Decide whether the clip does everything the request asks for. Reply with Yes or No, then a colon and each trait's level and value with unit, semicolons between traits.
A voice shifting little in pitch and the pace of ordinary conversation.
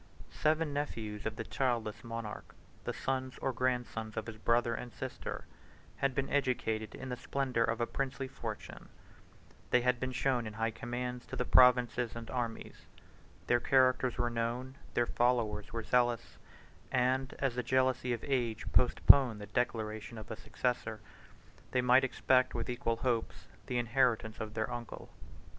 Yes: narrow, 2.1 semitones; average, 160 wpm